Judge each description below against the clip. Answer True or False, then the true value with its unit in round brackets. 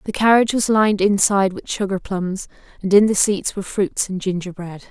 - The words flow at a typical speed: True (195 wpm)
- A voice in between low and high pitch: False (195 Hz)